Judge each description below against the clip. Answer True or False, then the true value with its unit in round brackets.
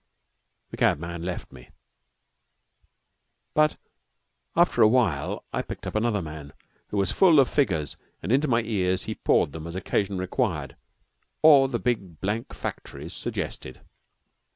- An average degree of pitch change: False (6.7 semitones)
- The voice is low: True (95 Hz)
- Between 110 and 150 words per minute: True (135 wpm)